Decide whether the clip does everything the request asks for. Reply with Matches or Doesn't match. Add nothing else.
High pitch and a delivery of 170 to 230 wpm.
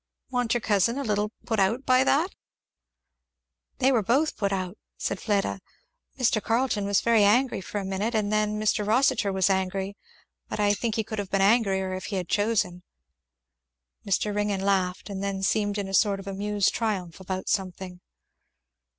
Matches